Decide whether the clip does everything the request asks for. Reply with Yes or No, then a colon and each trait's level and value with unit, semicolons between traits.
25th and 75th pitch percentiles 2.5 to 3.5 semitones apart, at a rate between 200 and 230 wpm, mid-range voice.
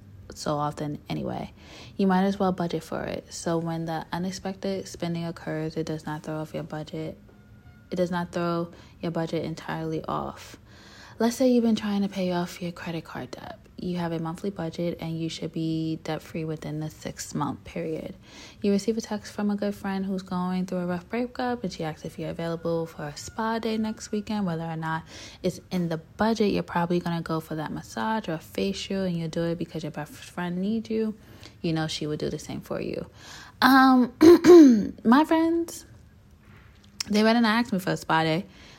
No: average, 4.3 semitones; fast, 205 wpm; medium, 170 Hz